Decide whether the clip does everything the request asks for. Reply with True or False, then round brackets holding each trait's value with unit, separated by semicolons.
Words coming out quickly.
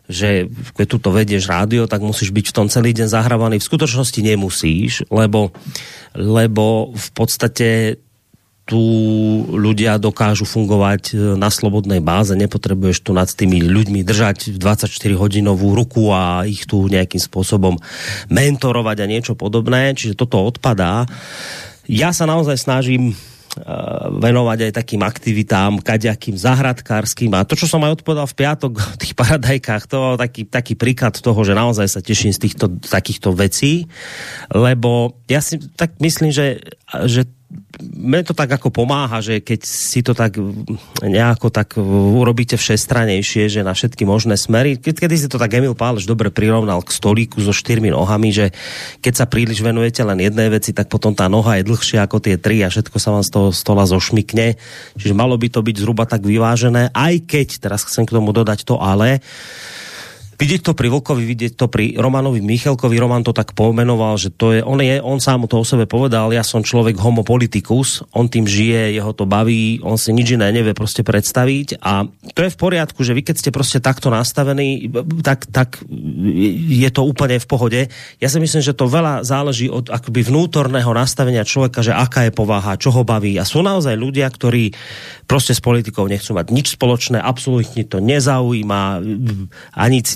True (175 wpm)